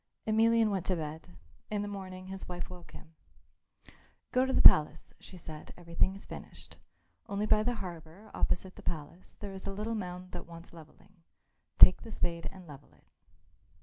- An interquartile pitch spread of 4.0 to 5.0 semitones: No, average, 3.3 semitones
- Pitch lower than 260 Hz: Yes, medium, 185 Hz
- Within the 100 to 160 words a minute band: No, average, 180 wpm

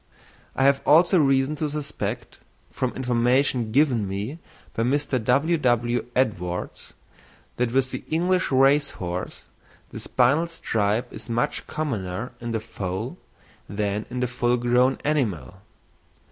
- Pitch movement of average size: Yes, average, 4.1 semitones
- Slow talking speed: Yes, slow, 130 wpm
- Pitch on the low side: Yes, low, 125 Hz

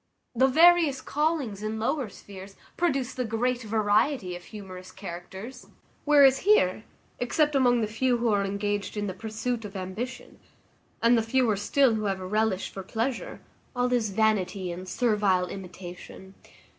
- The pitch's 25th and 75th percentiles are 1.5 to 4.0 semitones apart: No, average, 4.5 semitones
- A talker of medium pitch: No, high, 220 Hz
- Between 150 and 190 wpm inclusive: Yes, average, 155 wpm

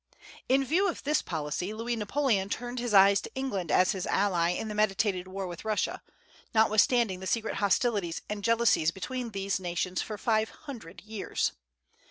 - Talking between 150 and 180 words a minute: Yes, average, 170 wpm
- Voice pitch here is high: Yes, high, 210 Hz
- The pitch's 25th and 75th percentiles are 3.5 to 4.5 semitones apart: Yes, average, 3.9 semitones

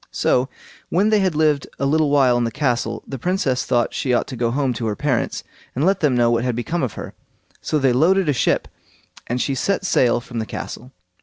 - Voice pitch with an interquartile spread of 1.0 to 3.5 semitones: No, average, 4.2 semitones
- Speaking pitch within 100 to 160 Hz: Yes, low, 135 Hz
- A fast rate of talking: Yes, fast, 230 wpm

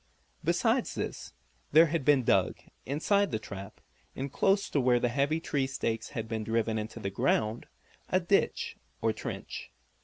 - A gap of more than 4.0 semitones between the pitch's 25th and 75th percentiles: Yes, wide, 5.6 semitones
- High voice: No, low, 130 Hz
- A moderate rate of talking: Yes, average, 160 wpm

